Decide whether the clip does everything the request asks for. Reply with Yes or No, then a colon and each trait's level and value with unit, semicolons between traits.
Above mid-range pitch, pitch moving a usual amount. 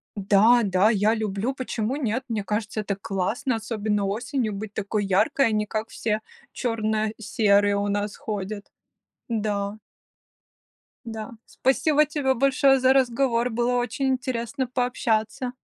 Yes: high, 220 Hz; average, 3.2 semitones